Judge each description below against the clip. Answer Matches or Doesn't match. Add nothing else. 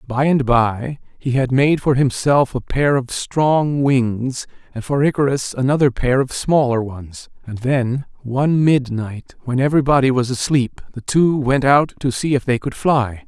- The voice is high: Doesn't match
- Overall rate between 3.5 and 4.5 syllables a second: Matches